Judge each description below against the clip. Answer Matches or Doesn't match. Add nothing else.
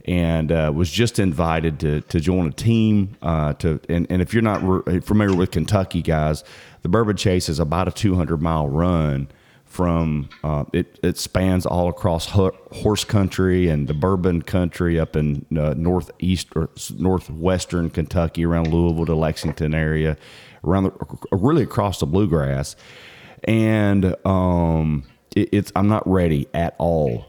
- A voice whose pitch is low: Matches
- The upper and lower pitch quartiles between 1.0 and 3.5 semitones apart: Matches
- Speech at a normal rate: Matches